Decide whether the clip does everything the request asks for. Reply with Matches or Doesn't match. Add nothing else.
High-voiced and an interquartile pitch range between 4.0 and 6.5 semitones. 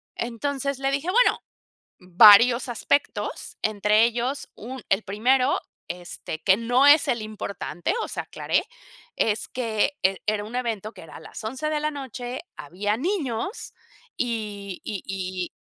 Matches